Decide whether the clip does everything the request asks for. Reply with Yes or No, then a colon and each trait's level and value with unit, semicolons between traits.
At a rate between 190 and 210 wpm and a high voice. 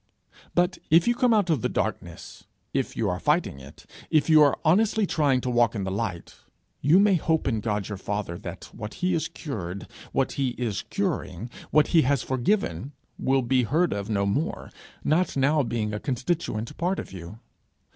No: average, 195 wpm; low, 130 Hz